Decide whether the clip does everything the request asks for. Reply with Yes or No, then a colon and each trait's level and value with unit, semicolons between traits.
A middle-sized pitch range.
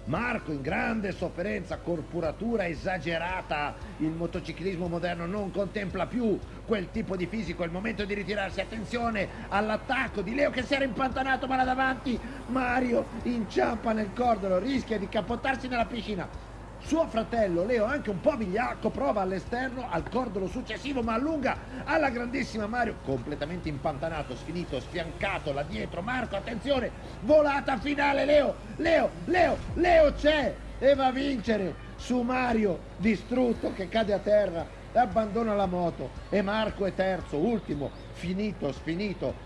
No: wide, 5.8 semitones